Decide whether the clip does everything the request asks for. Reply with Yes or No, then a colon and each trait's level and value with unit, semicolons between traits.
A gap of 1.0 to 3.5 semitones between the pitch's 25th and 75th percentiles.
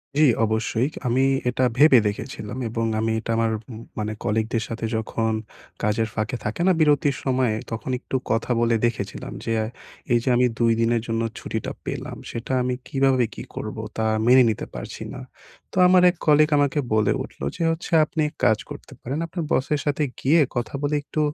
No: average, 4.2 semitones